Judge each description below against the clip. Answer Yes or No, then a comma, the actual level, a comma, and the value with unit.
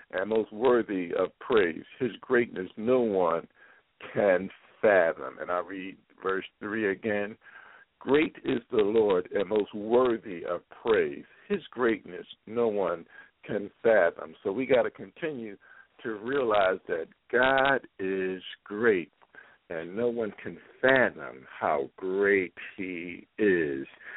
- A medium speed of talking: No, slow, 130 wpm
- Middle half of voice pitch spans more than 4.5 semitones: Yes, average, 5.3 semitones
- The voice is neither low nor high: No, low, 105 Hz